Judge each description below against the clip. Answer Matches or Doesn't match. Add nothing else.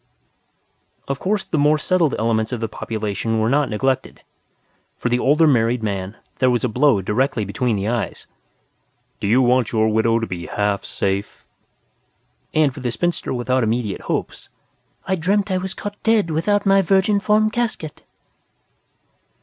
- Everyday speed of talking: Matches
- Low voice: Matches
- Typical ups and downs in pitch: Doesn't match